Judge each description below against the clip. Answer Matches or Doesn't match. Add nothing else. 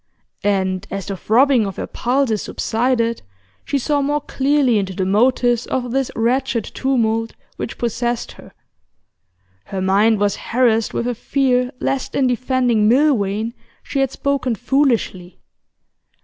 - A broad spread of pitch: Doesn't match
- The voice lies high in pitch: Matches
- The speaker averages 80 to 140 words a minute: Matches